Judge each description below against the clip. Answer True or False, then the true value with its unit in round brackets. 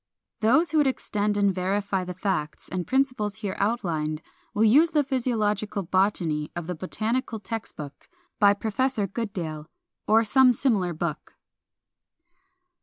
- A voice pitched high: True (205 Hz)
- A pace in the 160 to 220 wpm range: False (135 wpm)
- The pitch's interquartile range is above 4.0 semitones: True (4.4 semitones)